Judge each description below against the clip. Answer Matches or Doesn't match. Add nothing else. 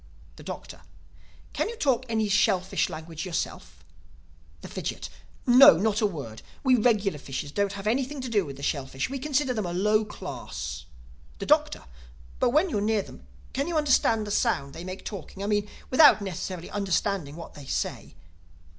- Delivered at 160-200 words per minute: Matches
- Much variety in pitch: Matches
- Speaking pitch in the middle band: Doesn't match